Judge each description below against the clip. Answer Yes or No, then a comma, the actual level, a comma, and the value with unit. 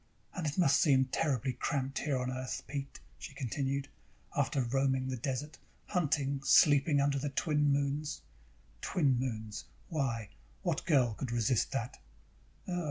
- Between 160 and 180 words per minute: No, average, 140 wpm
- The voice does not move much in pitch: Yes, narrow, 2.1 semitones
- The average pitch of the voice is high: No, low, 135 Hz